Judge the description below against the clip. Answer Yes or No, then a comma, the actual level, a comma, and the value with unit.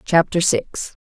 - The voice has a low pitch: No, medium, 160 Hz